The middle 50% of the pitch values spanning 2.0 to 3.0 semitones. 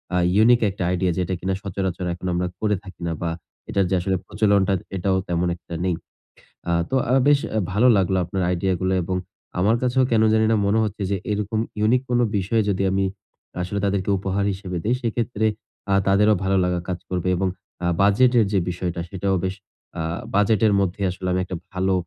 Yes: narrow, 2.5 semitones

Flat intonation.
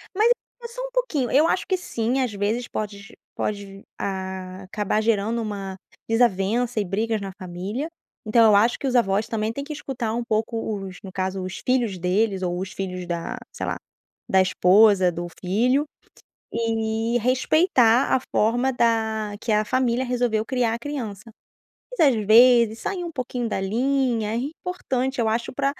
No: average, 3.9 semitones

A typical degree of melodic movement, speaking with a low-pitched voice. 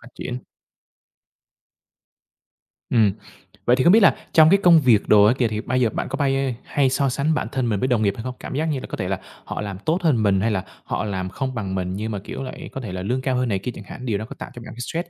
Yes: average, 4.6 semitones; low, 120 Hz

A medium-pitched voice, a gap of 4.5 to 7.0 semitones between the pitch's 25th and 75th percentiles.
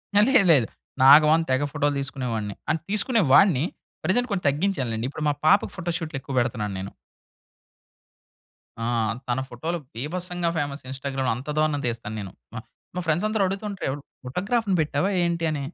Yes: medium, 150 Hz; wide, 5.6 semitones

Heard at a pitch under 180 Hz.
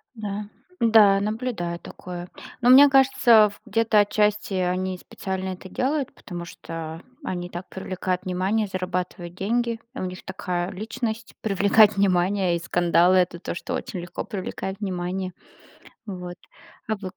No: high, 190 Hz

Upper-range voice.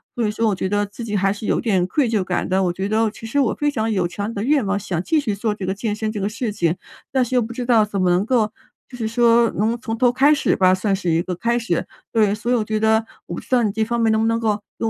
Yes: high, 220 Hz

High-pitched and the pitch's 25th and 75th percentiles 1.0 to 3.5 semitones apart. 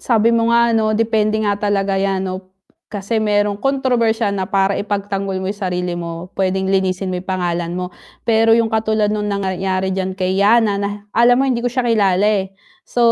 Yes: high, 200 Hz; average, 2.8 semitones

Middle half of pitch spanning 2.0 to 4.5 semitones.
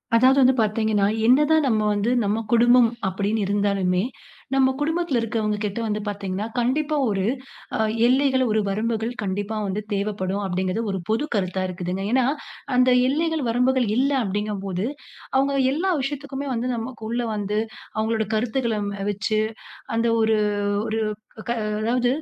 Yes: average, 4.0 semitones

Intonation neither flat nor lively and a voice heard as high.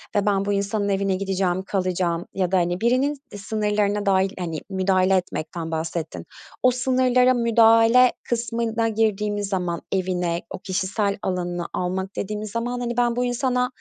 Yes: average, 3.9 semitones; high, 200 Hz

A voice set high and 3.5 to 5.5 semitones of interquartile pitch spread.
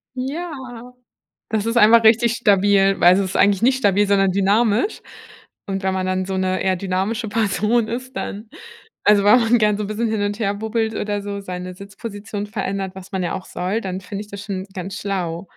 No: high, 205 Hz; average, 2.7 semitones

